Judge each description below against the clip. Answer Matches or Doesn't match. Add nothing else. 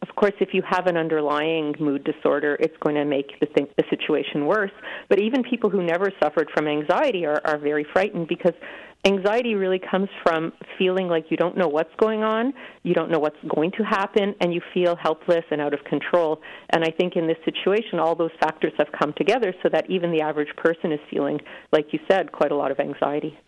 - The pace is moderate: Doesn't match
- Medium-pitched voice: Matches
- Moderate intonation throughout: Matches